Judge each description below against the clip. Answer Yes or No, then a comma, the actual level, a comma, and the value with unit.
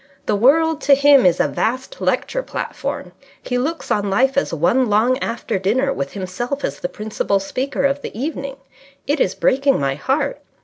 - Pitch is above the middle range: Yes, very high, 255 Hz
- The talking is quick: No, average, 180 wpm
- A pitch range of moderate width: No, wide, 5.8 semitones